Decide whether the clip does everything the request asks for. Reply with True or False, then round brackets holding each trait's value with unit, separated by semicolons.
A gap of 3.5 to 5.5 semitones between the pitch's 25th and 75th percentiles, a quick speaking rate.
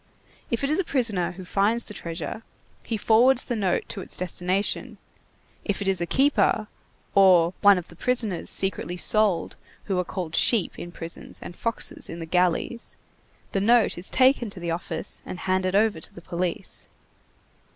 False (4.2 semitones; 175 wpm)